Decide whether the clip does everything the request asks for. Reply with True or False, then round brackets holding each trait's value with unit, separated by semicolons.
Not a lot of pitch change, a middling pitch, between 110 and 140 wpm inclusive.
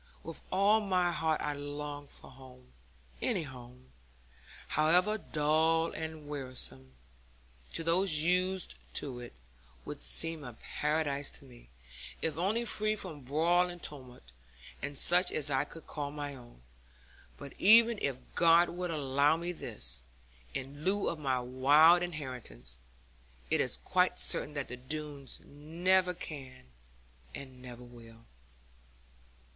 False (4.8 semitones; 150 Hz; 135 wpm)